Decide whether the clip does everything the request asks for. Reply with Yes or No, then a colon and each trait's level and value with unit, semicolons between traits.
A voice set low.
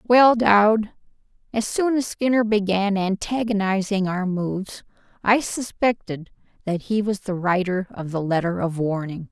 No: high, 200 Hz